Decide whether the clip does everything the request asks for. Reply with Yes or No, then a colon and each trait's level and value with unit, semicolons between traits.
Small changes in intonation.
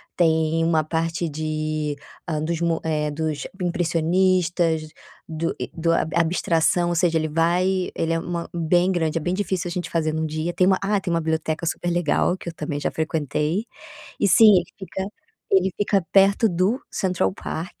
Yes: narrow, 2.3 semitones